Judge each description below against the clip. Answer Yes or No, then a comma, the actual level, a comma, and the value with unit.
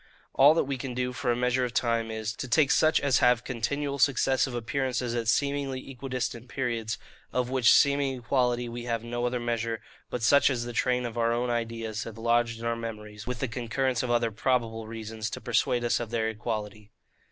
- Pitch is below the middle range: Yes, low, 120 Hz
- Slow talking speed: No, fast, 205 wpm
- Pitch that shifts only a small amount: Yes, narrow, 1.9 semitones